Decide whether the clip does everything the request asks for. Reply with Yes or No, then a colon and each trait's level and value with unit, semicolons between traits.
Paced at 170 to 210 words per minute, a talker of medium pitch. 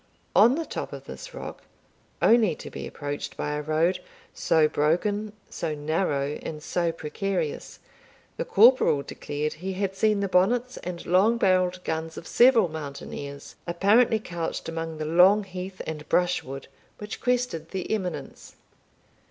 No: average, 145 wpm; medium, 180 Hz